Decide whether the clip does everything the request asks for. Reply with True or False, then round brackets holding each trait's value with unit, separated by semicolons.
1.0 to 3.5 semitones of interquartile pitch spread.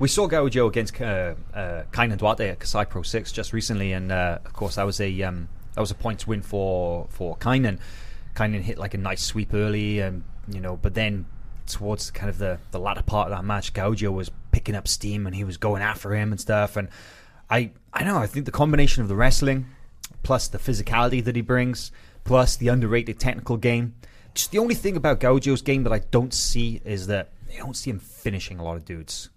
False (4.0 semitones)